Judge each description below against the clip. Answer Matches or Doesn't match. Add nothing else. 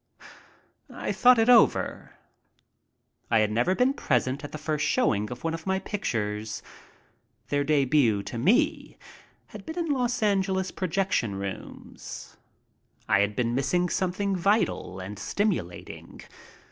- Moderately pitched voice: Matches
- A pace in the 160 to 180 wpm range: Doesn't match